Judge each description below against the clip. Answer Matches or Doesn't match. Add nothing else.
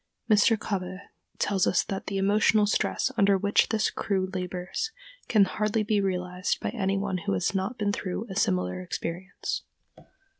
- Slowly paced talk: Doesn't match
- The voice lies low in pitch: Doesn't match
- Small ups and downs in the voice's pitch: Matches